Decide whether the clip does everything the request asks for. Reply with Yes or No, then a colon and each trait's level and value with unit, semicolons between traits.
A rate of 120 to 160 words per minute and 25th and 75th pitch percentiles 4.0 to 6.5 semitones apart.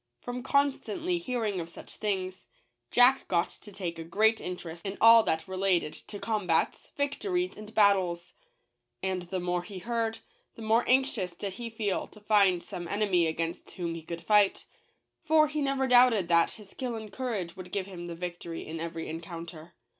No: average, 175 wpm; average, 5.0 semitones